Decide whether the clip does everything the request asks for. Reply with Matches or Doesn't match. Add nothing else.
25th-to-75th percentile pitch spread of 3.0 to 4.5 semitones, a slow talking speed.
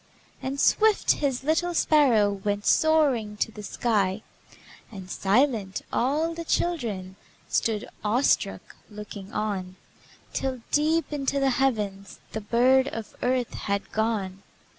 Doesn't match